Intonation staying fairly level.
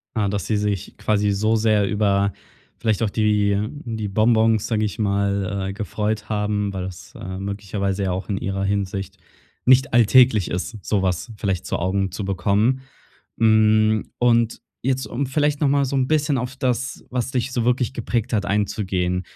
No: average, 3.1 semitones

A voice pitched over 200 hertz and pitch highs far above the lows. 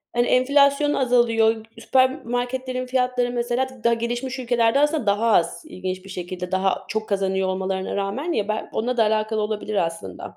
No: high, 230 Hz; average, 4.1 semitones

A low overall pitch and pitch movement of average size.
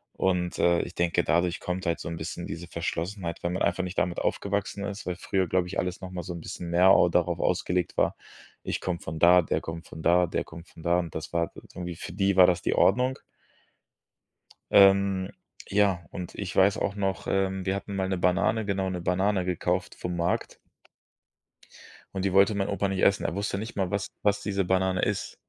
No: very low, 90 Hz; narrow, 2.0 semitones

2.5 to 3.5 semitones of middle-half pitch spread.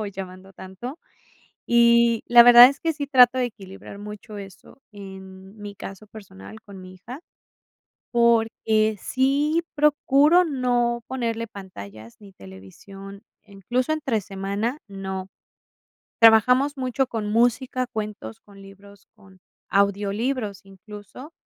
No: average, 4.2 semitones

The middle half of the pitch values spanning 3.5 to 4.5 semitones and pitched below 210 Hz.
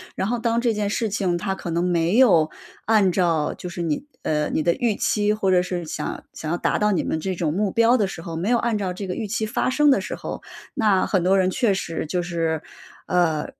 Yes: average, 3.9 semitones; high, 190 Hz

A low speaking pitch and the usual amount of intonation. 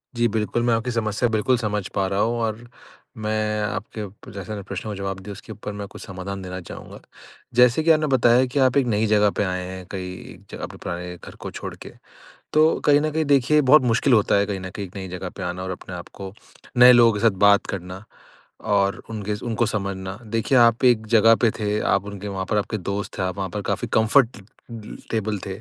Yes: low, 105 Hz; average, 3.2 semitones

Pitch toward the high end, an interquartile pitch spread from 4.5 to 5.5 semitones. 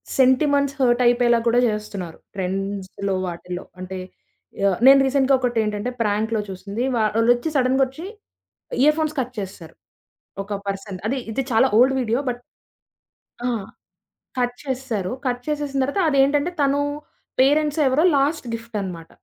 Yes: high, 245 Hz; average, 4.9 semitones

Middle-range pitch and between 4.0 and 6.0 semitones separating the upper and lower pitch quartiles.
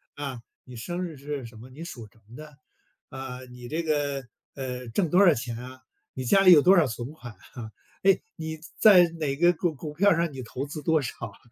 Yes: medium, 145 Hz; average, 4.8 semitones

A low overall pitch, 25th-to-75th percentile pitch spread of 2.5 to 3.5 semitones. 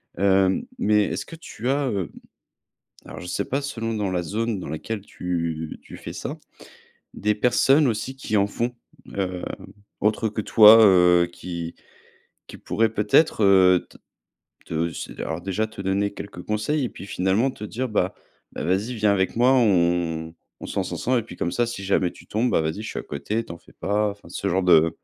No: low, 100 Hz; average, 4.0 semitones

